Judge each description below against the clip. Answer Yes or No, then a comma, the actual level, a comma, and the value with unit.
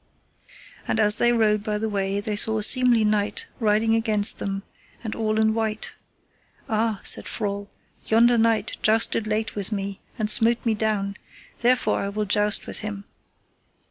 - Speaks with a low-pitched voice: No, high, 215 Hz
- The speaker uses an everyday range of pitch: No, narrow, 1.4 semitones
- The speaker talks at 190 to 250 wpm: No, average, 165 wpm